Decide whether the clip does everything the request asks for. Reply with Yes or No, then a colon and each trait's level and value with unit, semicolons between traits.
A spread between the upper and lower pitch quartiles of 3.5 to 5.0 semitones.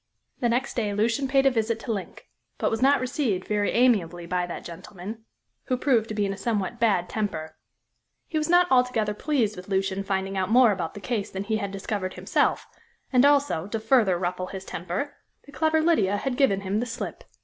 Yes: average, 4.6 semitones